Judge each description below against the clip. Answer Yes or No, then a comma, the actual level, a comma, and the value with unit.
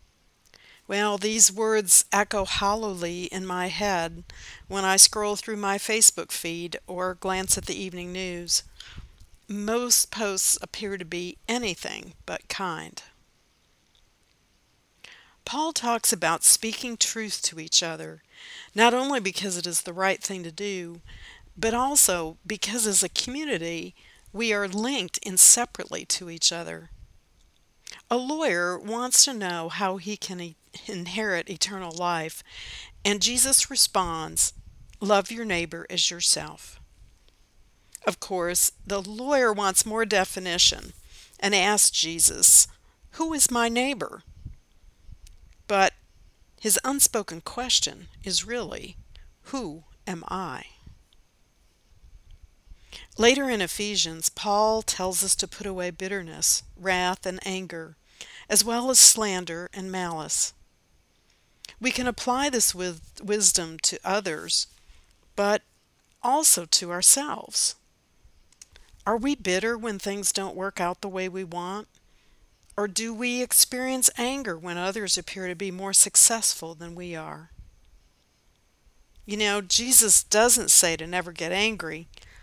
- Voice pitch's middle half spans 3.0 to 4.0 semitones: No, average, 4.4 semitones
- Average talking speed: No, slow, 125 wpm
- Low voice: No, high, 190 Hz